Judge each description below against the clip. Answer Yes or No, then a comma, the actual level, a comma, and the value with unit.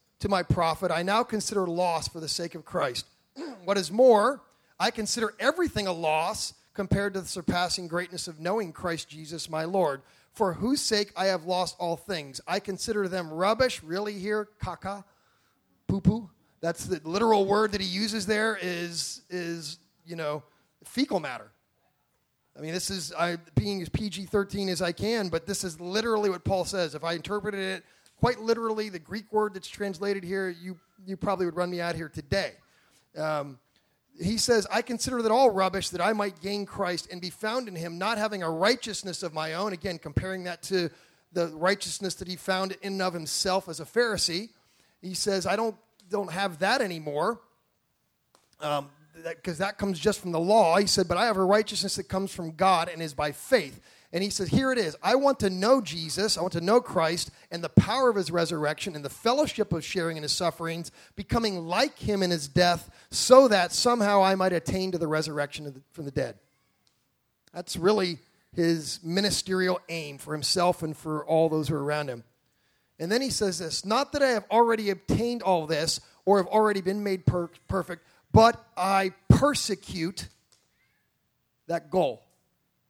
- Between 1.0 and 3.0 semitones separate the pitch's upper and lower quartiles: No, average, 3.6 semitones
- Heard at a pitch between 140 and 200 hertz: Yes, medium, 185 Hz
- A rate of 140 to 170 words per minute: No, average, 190 wpm